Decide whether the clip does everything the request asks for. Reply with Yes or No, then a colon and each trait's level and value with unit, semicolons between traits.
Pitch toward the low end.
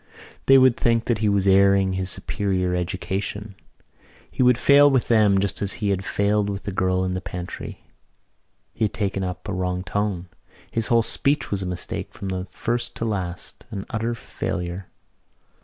Yes: low, 100 Hz